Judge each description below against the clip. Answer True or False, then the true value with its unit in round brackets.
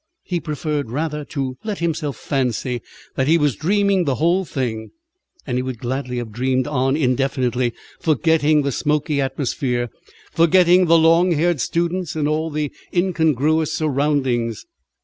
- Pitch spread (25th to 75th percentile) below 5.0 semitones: True (4.0 semitones)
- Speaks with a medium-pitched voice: True (150 Hz)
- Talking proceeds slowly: False (145 wpm)